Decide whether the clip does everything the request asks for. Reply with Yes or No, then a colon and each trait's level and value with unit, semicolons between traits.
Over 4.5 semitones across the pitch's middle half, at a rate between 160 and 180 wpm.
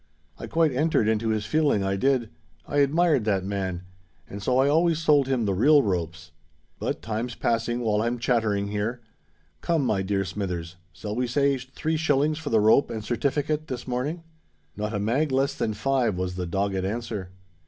Yes: wide, 5.6 semitones; average, 175 wpm